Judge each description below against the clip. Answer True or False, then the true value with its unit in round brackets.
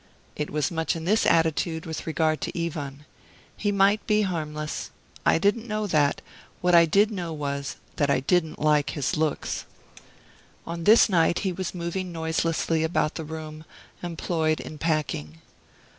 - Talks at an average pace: True (160 wpm)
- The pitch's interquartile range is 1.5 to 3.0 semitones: True (2.7 semitones)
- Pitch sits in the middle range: True (160 Hz)